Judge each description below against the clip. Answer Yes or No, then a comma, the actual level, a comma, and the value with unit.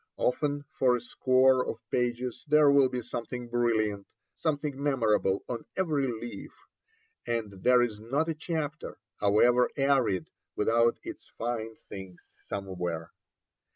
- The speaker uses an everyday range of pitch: Yes, average, 3.8 semitones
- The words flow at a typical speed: No, slow, 125 wpm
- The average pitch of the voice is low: Yes, low, 120 Hz